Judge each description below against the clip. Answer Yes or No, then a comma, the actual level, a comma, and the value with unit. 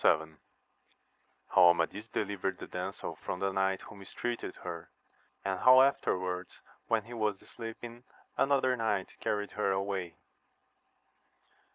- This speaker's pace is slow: Yes, slow, 125 wpm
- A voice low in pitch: Yes, low, 100 Hz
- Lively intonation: No, average, 3.5 semitones